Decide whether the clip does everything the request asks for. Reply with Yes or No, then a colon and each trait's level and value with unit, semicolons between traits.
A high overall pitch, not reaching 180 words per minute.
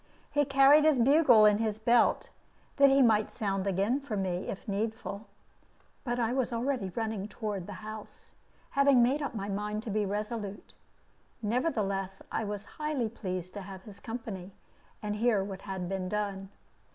Yes: high, 215 Hz; average, 165 wpm